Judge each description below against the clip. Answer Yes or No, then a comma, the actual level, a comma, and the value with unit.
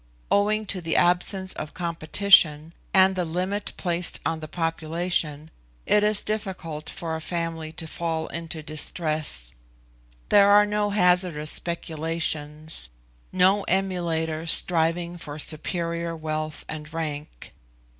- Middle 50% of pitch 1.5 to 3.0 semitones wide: Yes, average, 2.7 semitones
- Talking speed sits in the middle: No, slow, 120 wpm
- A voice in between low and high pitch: Yes, medium, 165 Hz